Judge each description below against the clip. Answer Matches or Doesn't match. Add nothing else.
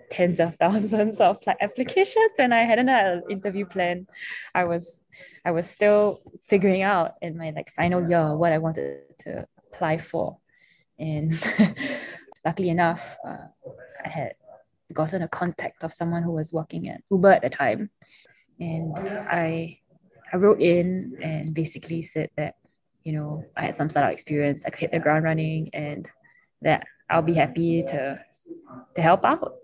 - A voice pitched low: Doesn't match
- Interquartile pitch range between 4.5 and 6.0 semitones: Doesn't match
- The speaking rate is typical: Matches